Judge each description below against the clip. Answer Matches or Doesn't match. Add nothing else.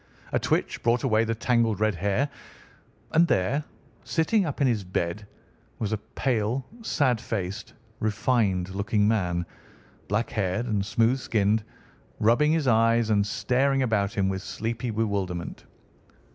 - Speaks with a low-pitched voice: Matches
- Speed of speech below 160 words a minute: Matches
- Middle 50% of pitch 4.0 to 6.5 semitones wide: Doesn't match